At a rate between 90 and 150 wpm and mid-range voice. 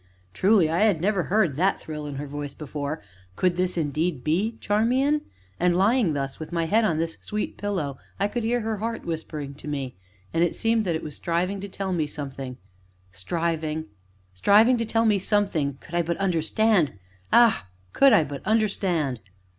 No: average, 185 wpm; medium, 175 Hz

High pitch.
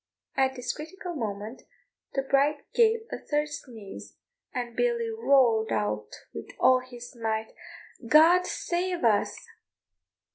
Yes: very high, 265 Hz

